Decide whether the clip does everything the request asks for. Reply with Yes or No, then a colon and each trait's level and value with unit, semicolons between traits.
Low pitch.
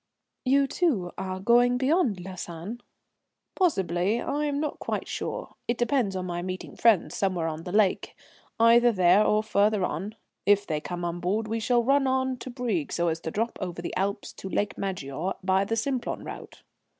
No: high, 205 Hz